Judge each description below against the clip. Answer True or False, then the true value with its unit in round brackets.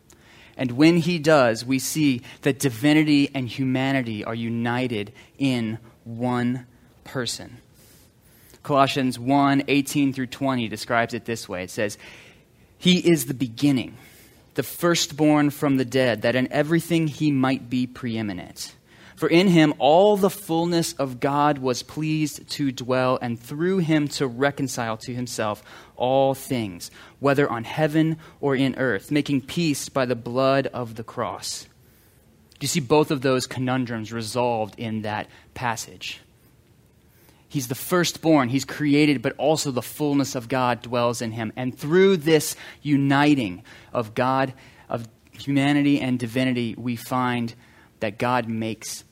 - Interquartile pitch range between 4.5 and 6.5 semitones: False (3.4 semitones)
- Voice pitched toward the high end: False (130 Hz)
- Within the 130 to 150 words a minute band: True (140 wpm)